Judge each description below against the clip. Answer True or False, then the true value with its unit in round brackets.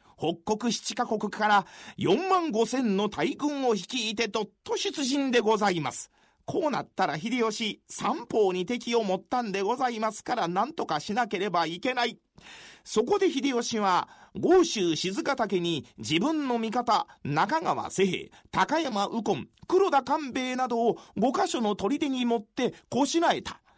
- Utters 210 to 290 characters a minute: True (280 characters per minute)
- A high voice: True (230 Hz)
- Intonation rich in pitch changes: False (5.0 semitones)